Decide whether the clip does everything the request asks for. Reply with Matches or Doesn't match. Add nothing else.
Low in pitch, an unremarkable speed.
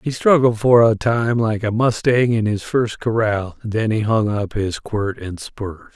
Doesn't match